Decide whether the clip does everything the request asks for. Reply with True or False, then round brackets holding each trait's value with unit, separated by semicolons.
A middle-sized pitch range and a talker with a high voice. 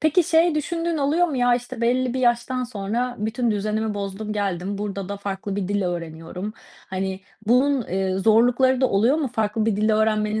True (4.1 semitones; 220 Hz)